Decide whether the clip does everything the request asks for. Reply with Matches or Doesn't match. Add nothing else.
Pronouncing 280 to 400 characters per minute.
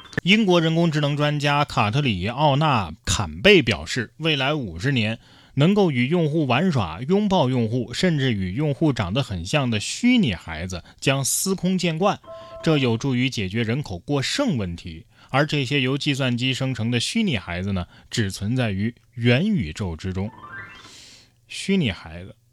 Doesn't match